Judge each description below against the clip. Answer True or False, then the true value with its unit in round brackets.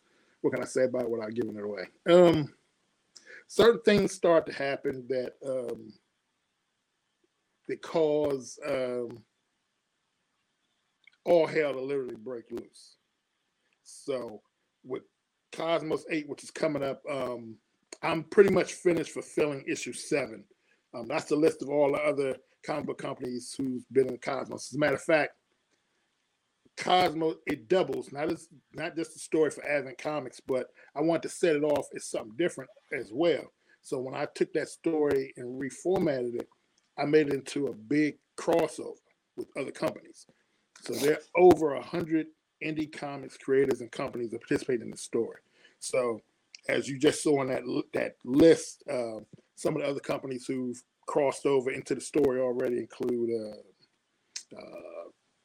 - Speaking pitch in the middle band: True (145 Hz)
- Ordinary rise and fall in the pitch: True (4.1 semitones)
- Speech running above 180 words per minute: False (160 wpm)